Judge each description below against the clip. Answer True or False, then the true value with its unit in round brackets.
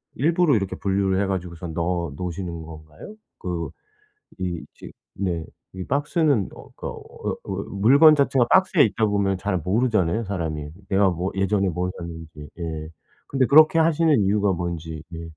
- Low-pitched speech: True (95 Hz)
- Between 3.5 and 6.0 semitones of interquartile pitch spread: True (5.5 semitones)